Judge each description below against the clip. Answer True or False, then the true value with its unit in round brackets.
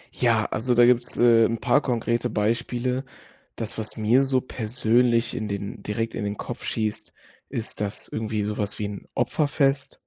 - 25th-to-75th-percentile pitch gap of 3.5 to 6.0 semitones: False (2.4 semitones)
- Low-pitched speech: True (115 Hz)